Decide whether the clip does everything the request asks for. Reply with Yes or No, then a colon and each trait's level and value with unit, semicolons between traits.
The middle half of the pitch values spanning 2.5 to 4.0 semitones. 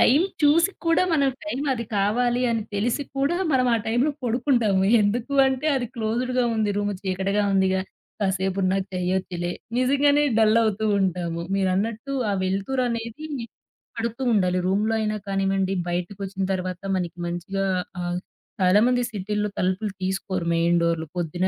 No: average, 4.5 semitones